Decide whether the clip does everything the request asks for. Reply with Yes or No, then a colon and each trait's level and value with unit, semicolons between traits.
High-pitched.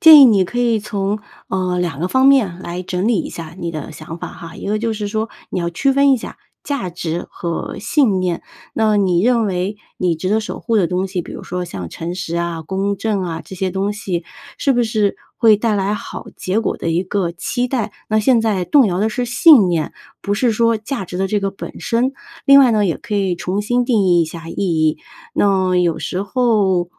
Yes: high, 195 Hz